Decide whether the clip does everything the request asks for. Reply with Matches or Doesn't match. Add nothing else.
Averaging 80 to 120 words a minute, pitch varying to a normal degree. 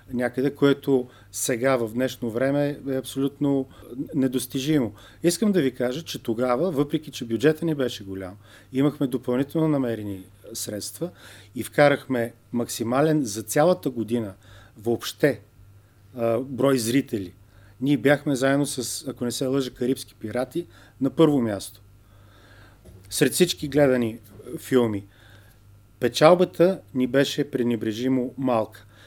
Matches